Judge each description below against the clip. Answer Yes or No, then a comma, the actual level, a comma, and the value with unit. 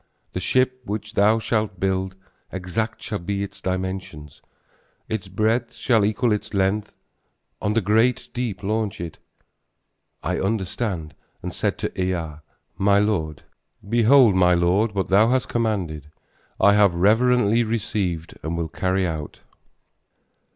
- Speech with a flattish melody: No, average, 3.2 semitones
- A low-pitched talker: Yes, low, 100 Hz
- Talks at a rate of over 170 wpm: No, slow, 135 wpm